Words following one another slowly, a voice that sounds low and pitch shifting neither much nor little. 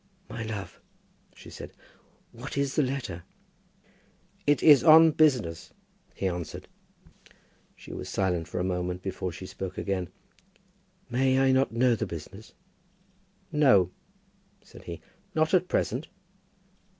No: slow, 125 wpm; low, 115 Hz; wide, 7.0 semitones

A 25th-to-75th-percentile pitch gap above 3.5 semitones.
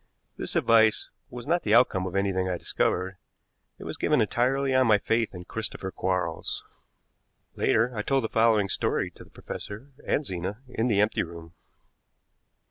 Yes: average, 4.6 semitones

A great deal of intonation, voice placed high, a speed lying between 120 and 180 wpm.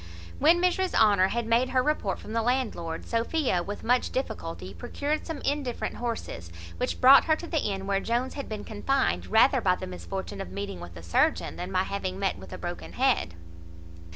No: wide, 5.7 semitones; high, 225 Hz; average, 195 wpm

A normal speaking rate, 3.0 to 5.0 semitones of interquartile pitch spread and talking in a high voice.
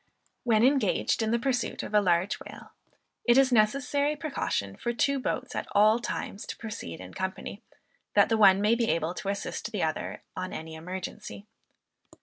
Yes: average, 180 wpm; average, 4.5 semitones; high, 215 Hz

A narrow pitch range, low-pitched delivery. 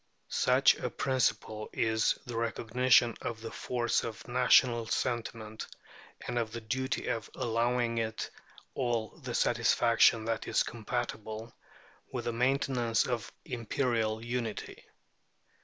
Yes: narrow, 1.7 semitones; low, 115 Hz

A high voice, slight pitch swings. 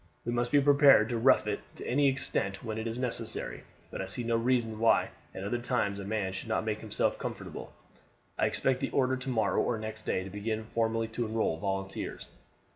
No: low, 115 Hz; narrow, 2.3 semitones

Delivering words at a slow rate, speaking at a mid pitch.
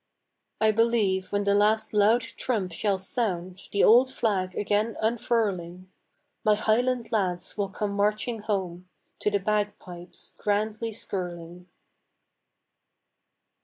No: slow, 115 wpm; high, 205 Hz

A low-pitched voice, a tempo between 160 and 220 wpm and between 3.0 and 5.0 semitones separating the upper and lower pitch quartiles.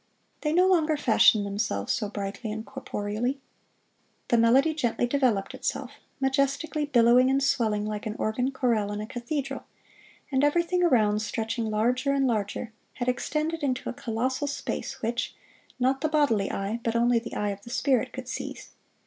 No: high, 245 Hz; average, 165 wpm; average, 4.2 semitones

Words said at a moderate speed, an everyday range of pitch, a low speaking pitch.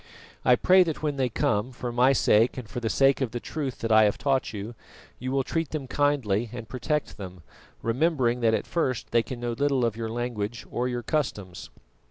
No: fast, 215 wpm; average, 3.3 semitones; low, 125 Hz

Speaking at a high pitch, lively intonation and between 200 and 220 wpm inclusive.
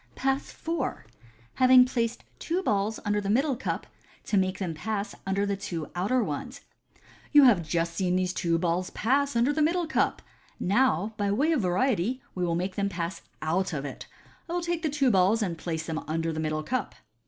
Yes: high, 200 Hz; wide, 6.7 semitones; fast, 205 wpm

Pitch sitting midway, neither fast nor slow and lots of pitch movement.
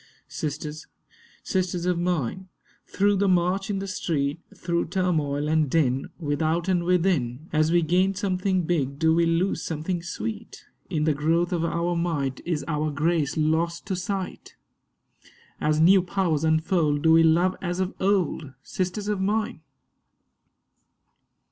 No: medium, 170 Hz; average, 145 wpm; average, 3.1 semitones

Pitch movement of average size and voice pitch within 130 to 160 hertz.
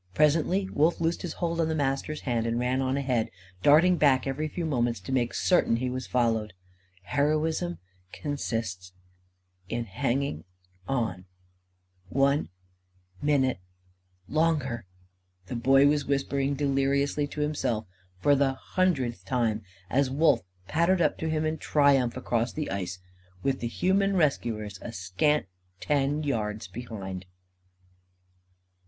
Yes: average, 4.5 semitones; low, 135 Hz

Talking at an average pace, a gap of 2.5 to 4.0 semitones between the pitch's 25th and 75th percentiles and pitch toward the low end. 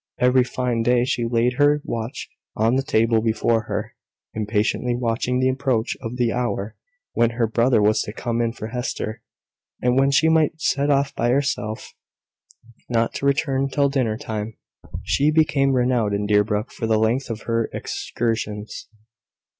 Yes: average, 160 wpm; average, 3.1 semitones; low, 120 Hz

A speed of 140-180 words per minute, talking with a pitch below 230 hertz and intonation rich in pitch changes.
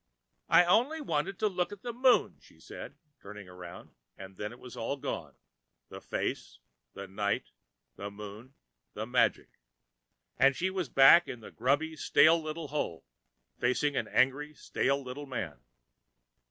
Yes: average, 155 wpm; medium, 140 Hz; wide, 7.9 semitones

